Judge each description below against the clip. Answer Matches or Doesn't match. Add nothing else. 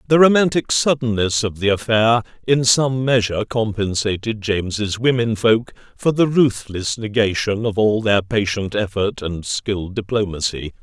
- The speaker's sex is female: Doesn't match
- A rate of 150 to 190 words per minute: Doesn't match